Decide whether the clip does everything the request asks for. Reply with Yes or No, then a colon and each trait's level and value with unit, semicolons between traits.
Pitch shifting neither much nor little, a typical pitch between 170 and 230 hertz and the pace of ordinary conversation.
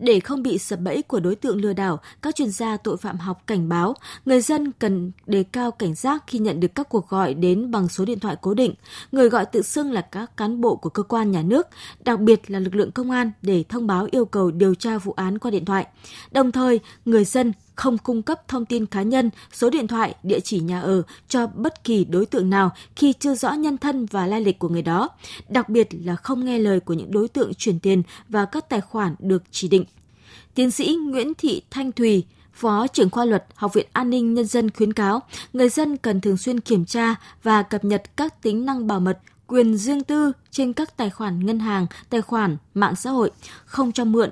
Yes: average, 4.3 semitones; high, 220 Hz; average, 235 wpm